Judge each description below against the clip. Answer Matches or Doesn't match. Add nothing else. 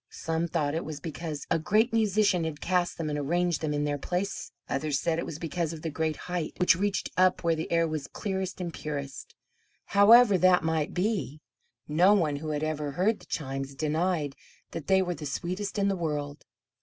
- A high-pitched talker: Doesn't match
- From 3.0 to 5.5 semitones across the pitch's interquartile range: Matches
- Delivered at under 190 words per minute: Doesn't match